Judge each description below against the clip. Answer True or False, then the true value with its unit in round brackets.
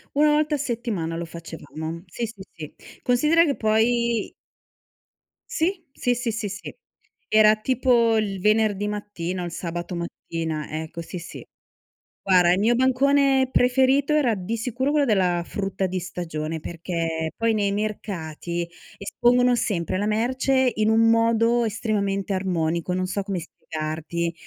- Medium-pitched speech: False (210 Hz)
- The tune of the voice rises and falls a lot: True (5.7 semitones)